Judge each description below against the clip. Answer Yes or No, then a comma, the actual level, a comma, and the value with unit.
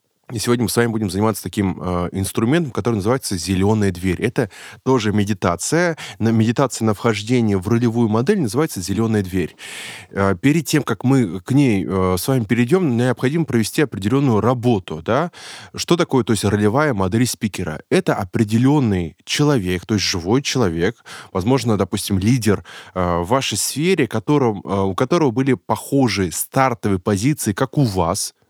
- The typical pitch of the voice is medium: No, low, 115 Hz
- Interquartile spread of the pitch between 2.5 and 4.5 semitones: No, average, 5.0 semitones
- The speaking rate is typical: Yes, average, 145 wpm